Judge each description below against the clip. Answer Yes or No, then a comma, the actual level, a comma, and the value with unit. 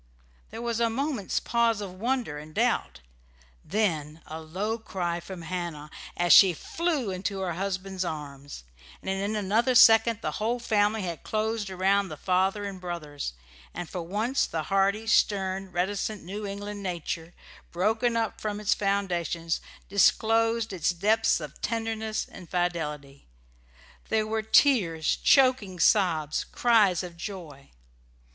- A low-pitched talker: No, high, 195 Hz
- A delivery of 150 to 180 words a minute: No, average, 140 wpm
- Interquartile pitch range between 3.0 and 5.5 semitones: Yes, average, 4.2 semitones